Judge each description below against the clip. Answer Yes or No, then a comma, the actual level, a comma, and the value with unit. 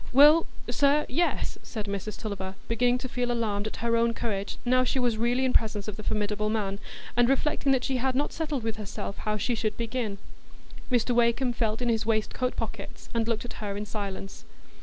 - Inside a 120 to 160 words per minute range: No, average, 200 wpm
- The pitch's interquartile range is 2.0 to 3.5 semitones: Yes, average, 2.9 semitones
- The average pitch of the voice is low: No, high, 230 Hz